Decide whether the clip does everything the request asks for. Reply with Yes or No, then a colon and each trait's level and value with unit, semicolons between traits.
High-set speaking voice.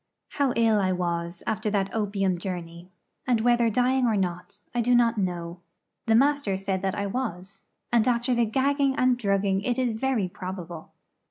Yes: high, 210 Hz